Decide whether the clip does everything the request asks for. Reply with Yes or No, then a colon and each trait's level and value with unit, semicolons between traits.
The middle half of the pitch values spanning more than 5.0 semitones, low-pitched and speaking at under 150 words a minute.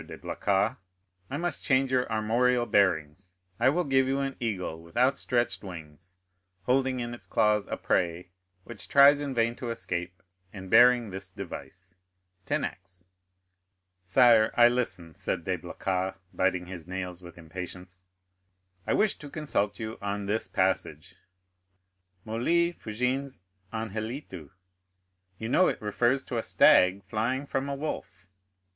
Yes: wide, 5.5 semitones; low, 110 Hz; average, 140 wpm